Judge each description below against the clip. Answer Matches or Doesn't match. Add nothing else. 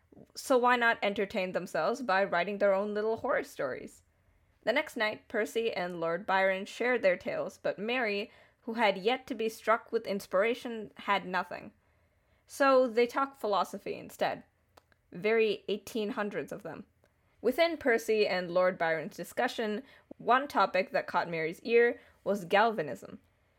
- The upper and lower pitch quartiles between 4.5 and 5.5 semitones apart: Doesn't match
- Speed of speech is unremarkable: Matches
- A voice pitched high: Matches